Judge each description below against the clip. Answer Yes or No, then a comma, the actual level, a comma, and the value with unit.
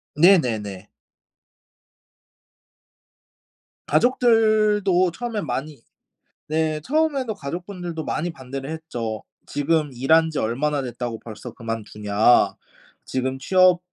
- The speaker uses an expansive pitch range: Yes, wide, 6.7 semitones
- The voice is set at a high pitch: No, medium, 155 Hz